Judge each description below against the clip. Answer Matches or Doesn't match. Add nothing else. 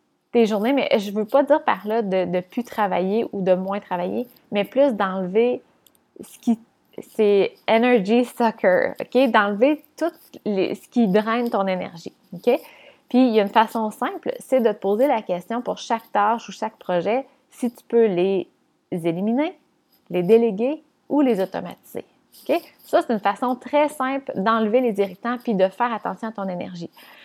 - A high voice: Matches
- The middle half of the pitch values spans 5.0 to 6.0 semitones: Doesn't match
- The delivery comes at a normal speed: Matches